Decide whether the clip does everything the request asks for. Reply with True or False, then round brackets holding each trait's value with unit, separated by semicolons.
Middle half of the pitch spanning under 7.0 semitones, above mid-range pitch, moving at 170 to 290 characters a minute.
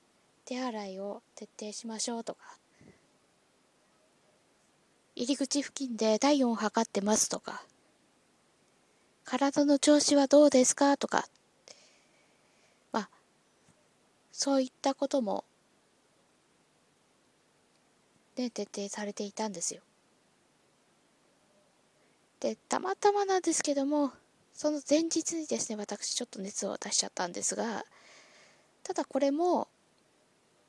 True (5.1 semitones; 270 Hz; 205 characters per minute)